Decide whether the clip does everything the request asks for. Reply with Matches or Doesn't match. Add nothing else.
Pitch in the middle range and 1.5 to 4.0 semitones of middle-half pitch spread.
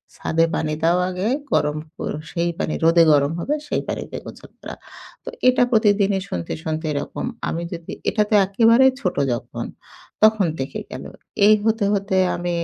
Doesn't match